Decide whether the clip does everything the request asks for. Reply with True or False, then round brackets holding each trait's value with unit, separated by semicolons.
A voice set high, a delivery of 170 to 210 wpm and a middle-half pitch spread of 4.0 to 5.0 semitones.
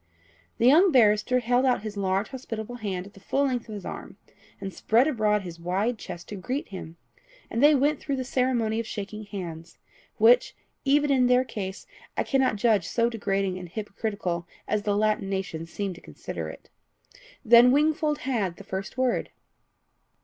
True (215 Hz; 180 wpm; 4.4 semitones)